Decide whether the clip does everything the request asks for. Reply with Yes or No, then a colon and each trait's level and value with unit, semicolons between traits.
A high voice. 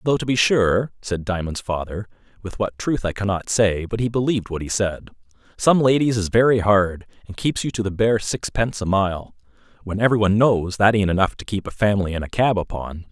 No: low, 105 Hz